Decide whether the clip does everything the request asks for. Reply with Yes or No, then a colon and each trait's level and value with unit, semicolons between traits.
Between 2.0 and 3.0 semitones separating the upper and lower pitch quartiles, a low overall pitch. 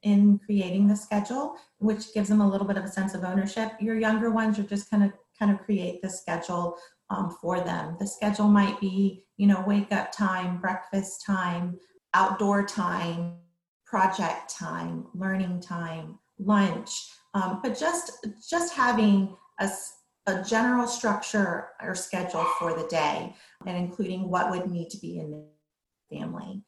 No: narrow, 2.6 semitones; high, 195 Hz